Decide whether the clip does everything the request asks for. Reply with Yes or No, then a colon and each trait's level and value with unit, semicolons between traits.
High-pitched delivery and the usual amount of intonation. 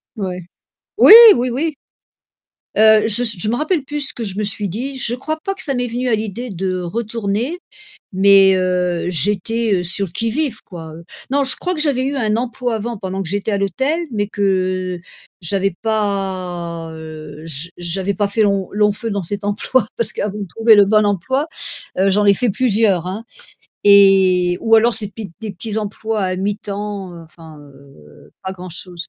Yes: high, 205 Hz; average, 3.8 semitones